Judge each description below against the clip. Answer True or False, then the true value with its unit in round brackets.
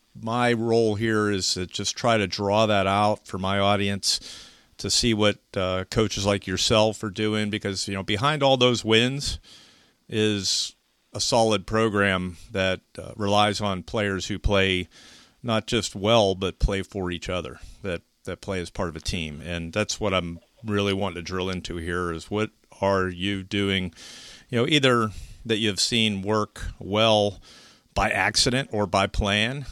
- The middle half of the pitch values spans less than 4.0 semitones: True (2.9 semitones)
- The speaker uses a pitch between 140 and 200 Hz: False (100 Hz)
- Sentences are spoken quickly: False (170 wpm)